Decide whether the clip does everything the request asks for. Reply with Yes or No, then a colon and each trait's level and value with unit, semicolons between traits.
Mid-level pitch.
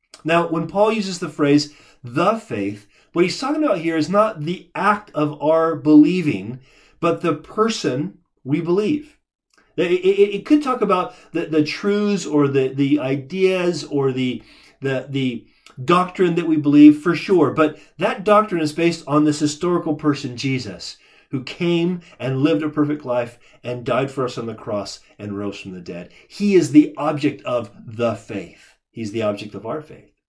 Yes: medium, 155 Hz